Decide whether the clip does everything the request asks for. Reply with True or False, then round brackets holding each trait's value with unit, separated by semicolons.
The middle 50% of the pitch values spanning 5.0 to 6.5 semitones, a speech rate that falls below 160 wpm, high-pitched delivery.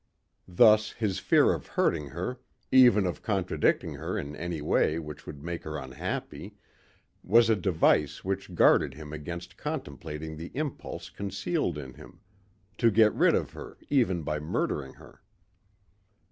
False (5.3 semitones; 145 wpm; 85 Hz)